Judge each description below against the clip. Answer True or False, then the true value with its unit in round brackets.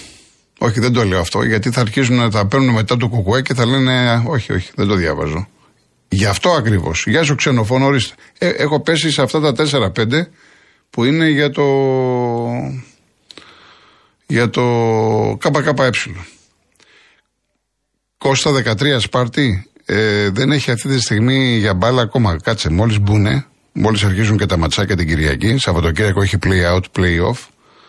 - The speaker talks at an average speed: True (150 wpm)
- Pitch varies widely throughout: False (4.6 semitones)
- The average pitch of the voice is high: False (120 Hz)